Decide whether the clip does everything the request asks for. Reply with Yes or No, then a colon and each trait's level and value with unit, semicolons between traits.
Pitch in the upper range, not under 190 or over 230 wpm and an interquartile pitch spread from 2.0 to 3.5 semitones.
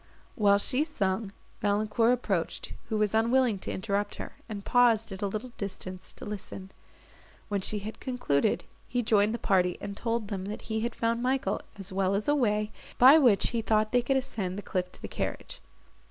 Yes: high, 215 Hz; average, 195 wpm; average, 3.1 semitones